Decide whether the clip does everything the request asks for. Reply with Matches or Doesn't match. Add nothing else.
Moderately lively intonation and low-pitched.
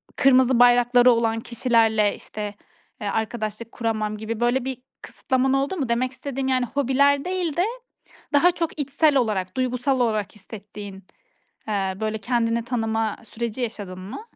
Doesn't match